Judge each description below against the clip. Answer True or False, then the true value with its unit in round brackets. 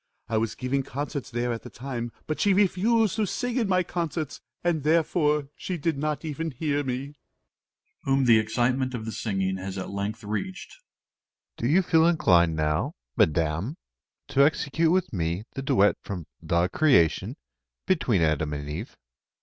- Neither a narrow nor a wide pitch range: False (8.1 semitones)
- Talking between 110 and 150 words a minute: False (170 wpm)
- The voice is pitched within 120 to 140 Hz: True (135 Hz)